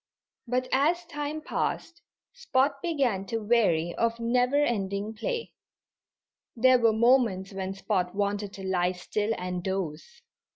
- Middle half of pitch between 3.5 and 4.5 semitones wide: No, wide, 5.5 semitones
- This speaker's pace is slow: Yes, slow, 130 wpm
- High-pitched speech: Yes, high, 225 Hz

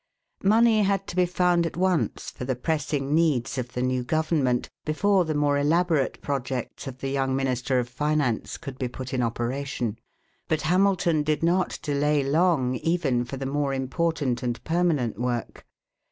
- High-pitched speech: No, medium, 145 Hz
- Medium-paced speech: Yes, average, 170 wpm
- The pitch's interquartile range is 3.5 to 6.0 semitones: Yes, average, 4.7 semitones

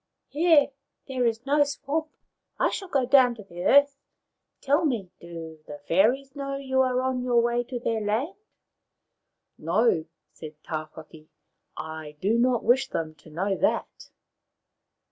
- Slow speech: No, average, 160 wpm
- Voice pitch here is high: Yes, high, 240 Hz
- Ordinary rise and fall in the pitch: No, wide, 8.1 semitones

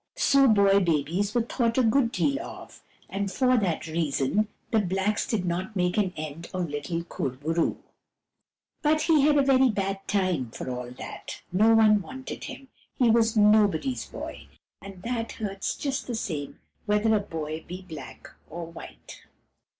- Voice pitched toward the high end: Yes, high, 200 Hz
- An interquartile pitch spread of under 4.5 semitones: No, wide, 5.4 semitones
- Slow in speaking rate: No, average, 170 wpm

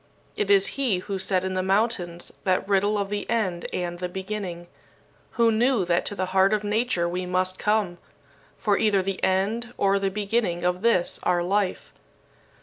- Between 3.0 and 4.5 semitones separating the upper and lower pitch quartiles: No, narrow, 2.5 semitones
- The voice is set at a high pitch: Yes, high, 195 Hz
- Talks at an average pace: Yes, average, 180 wpm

